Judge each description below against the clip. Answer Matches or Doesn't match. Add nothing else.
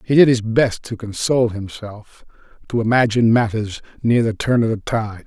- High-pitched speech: Doesn't match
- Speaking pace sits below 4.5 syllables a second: Doesn't match